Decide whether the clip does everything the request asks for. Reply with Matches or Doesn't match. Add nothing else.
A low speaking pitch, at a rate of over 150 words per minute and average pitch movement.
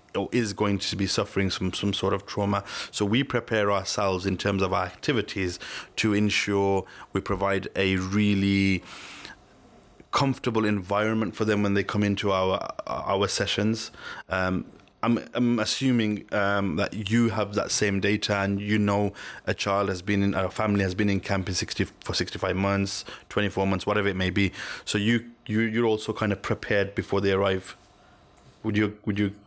Doesn't match